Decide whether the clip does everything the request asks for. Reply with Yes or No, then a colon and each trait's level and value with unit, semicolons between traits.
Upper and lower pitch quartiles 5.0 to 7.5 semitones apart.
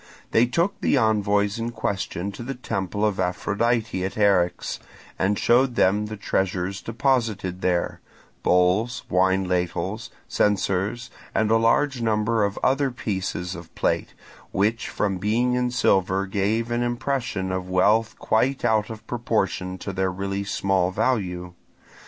No: average, 3.8 semitones